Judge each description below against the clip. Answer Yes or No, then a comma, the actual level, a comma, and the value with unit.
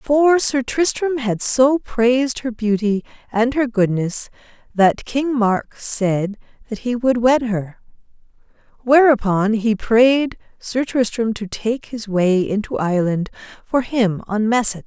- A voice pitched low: No, high, 230 Hz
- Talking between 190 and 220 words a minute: No, average, 140 wpm